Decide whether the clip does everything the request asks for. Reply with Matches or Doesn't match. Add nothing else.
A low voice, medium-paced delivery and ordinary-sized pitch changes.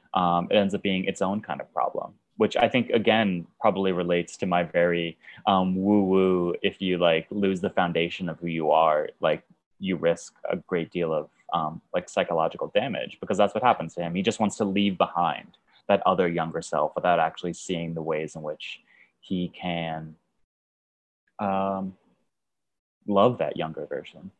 Doesn't match